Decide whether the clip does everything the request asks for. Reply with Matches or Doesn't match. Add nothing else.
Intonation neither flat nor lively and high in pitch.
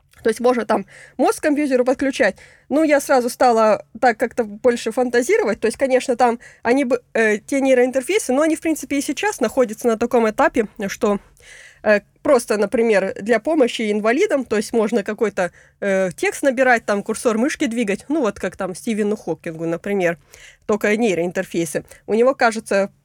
Matches